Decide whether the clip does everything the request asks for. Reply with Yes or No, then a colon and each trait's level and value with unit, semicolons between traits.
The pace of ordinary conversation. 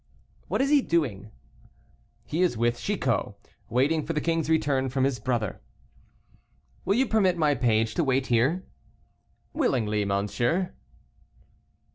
No: slow, 130 wpm